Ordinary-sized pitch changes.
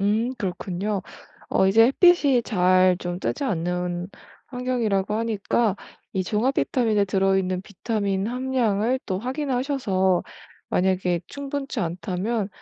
Yes: average, 4.9 semitones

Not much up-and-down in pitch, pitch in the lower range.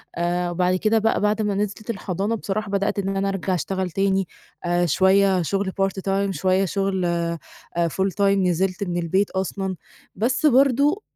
No: narrow, 1.7 semitones; high, 195 Hz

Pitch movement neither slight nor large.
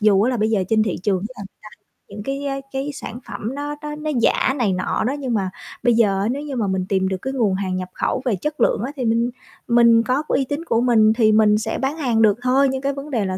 Yes: average, 4.5 semitones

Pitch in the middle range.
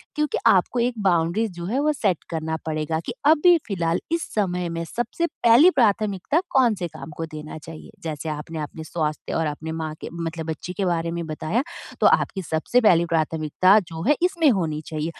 Yes: medium, 170 Hz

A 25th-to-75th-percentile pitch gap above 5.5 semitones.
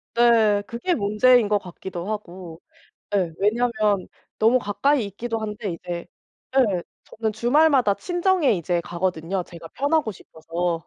No: average, 5.2 semitones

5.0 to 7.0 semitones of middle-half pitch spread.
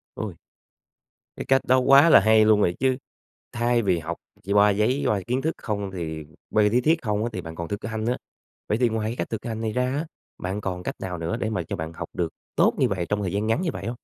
No: average, 4.3 semitones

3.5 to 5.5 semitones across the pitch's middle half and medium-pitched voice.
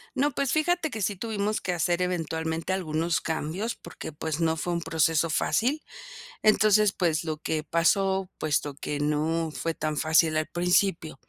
Yes: average, 4.0 semitones; medium, 165 Hz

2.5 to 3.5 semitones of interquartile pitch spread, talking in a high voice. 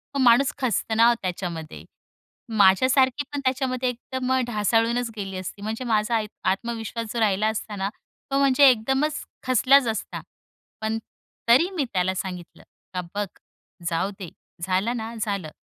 No: average, 4.5 semitones; high, 225 Hz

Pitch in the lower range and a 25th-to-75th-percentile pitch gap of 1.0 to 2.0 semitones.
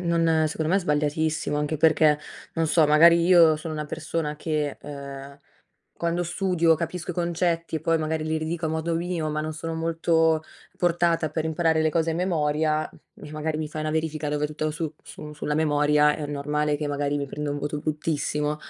No: medium, 155 Hz; narrow, 1.7 semitones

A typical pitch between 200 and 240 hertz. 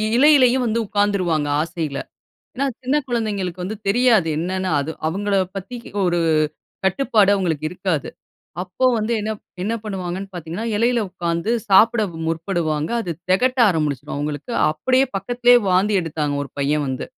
No: high, 190 Hz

